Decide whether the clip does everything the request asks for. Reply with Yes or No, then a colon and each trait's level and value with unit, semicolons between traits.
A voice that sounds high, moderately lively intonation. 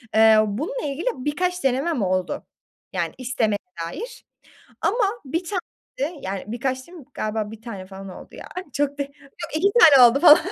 No: very high, 270 Hz; wide, 7.1 semitones